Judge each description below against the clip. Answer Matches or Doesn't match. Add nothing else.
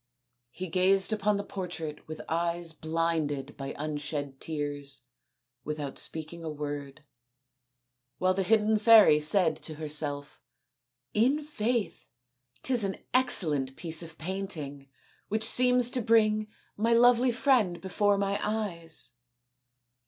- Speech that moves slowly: Matches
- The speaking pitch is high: Doesn't match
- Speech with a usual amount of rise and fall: Doesn't match